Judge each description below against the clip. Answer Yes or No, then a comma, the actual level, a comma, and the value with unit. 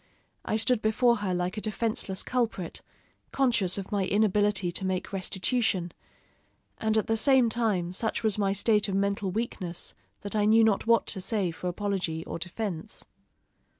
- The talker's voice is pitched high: Yes, high, 205 Hz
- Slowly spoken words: No, average, 165 wpm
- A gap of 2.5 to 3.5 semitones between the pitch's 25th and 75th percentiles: Yes, average, 2.9 semitones